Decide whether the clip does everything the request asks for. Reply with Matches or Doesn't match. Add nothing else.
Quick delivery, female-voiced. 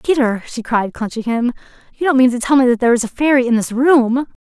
Matches